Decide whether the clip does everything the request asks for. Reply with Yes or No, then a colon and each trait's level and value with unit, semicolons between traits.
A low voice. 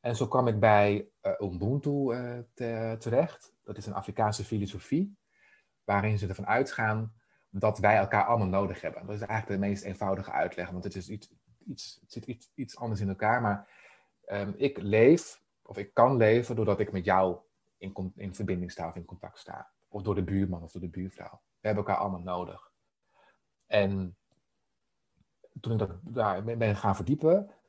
Yes: low, 105 Hz